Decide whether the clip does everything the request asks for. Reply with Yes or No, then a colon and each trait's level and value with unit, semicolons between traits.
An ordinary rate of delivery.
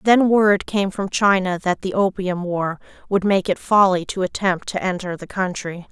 Yes: average, 195 wpm